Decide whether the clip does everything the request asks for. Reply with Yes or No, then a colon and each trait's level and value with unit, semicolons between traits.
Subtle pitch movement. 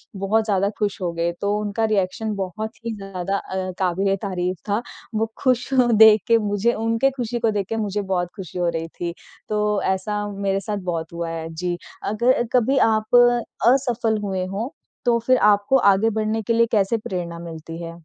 No: average, 3.3 semitones